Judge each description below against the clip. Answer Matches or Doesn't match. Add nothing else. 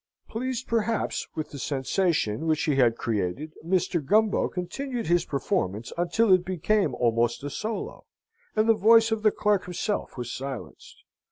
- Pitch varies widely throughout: Matches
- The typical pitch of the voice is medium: Matches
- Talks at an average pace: Matches